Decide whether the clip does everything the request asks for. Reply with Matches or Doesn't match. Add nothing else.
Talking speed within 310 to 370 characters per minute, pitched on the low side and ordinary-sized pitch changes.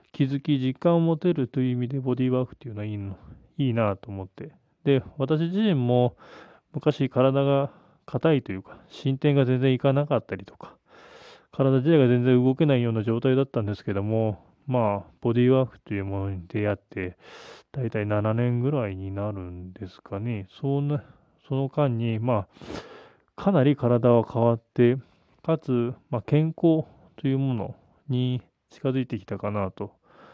Matches